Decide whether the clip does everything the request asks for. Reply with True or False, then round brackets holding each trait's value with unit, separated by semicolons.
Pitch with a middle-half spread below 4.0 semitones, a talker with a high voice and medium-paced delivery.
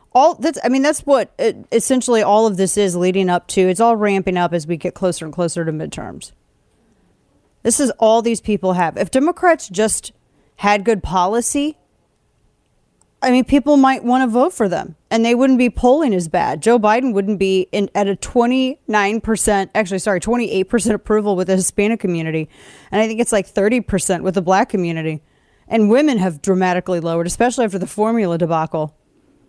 False (4.3 semitones; 210 Hz; 185 wpm)